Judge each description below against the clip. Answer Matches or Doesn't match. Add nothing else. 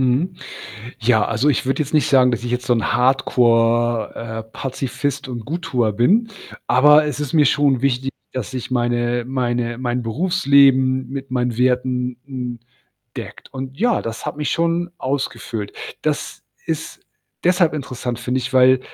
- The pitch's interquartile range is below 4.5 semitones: Matches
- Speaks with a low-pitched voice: Matches